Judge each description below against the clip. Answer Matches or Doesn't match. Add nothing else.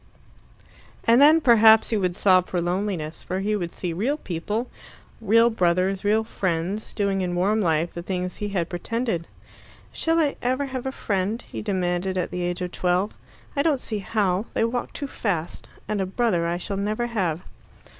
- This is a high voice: Matches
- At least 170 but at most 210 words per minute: Matches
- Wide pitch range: Doesn't match